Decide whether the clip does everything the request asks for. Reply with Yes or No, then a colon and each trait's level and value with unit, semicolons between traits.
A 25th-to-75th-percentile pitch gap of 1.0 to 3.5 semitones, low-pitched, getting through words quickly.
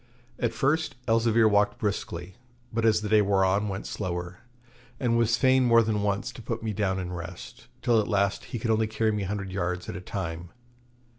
Yes: average, 3.2 semitones; low, 105 Hz; fast, 210 wpm